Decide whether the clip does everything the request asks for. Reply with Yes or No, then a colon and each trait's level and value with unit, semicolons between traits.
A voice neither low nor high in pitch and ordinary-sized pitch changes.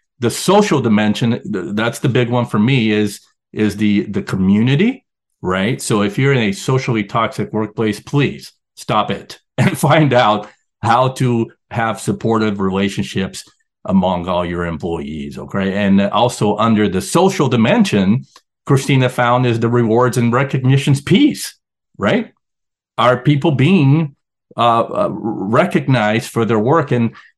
No: low, 115 Hz; average, 4.6 semitones